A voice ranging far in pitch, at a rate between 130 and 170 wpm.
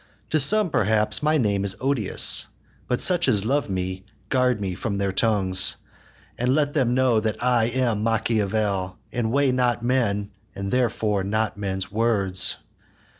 No: average, 4.1 semitones; average, 155 wpm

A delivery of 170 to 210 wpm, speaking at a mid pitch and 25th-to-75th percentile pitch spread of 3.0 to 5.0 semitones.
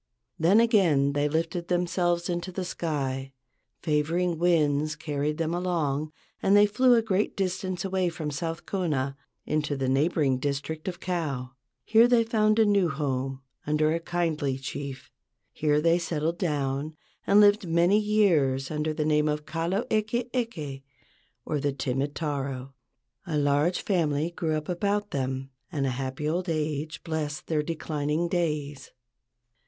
No: average, 150 wpm; medium, 155 Hz; average, 3.8 semitones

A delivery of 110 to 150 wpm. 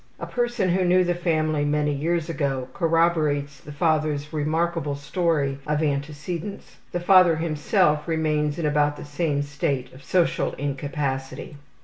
Yes: average, 140 wpm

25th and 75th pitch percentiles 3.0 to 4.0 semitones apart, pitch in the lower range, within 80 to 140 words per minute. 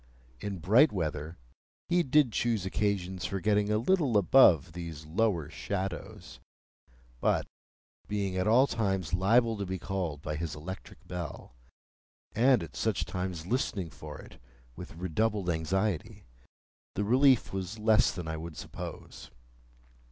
No: average, 4.6 semitones; very low, 95 Hz; slow, 135 wpm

